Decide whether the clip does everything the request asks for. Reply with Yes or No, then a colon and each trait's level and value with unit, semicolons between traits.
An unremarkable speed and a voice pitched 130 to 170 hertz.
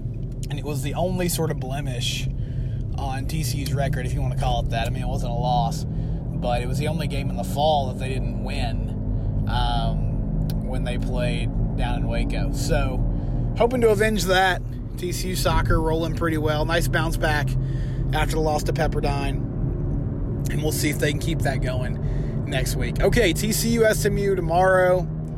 Yes: average, 180 wpm; low, 135 Hz